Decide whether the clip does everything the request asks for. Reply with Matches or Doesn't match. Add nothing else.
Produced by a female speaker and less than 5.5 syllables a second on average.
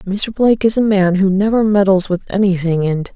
Matches